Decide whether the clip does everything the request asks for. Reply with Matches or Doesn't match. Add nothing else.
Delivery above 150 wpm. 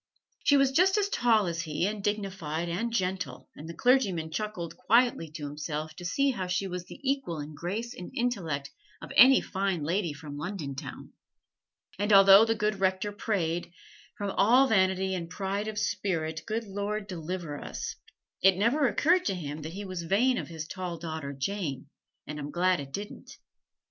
Matches